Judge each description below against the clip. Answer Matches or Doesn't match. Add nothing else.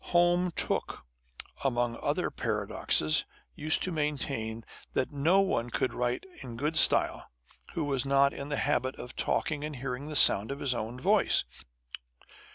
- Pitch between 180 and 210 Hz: Doesn't match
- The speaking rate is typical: Matches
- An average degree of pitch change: Matches